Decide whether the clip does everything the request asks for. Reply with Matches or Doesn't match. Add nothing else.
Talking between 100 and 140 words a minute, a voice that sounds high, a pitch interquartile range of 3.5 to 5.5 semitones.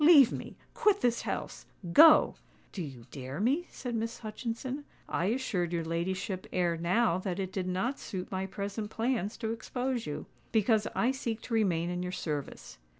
Doesn't match